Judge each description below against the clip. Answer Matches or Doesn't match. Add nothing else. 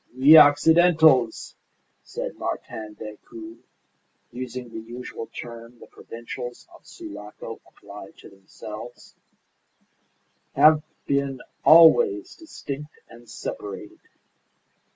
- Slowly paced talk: Matches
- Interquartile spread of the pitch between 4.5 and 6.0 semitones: Matches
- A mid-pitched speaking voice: Doesn't match